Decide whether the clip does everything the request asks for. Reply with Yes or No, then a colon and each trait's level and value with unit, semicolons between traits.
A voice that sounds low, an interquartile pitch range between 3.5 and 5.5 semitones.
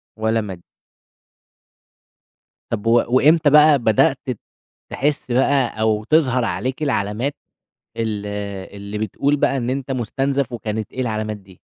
Yes: low, 120 Hz; average, 4.2 semitones